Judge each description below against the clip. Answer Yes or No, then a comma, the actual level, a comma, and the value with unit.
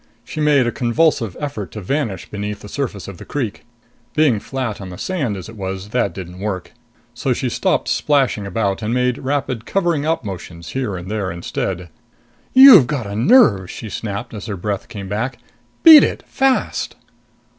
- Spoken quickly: No, average, 180 wpm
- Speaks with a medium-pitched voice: No, low, 110 Hz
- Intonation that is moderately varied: No, wide, 6.0 semitones